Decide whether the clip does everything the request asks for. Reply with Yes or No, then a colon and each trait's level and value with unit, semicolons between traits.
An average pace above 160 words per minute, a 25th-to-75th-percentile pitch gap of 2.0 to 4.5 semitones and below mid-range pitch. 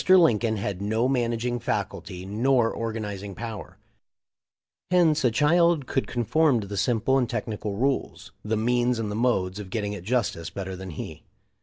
Yes: average, 170 wpm; average, 3.6 semitones; low, 115 Hz